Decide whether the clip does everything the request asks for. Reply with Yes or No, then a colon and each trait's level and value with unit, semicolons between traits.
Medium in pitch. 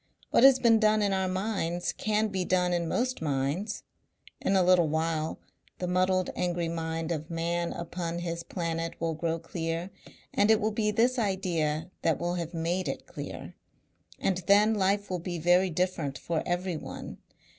Yes: medium, 175 Hz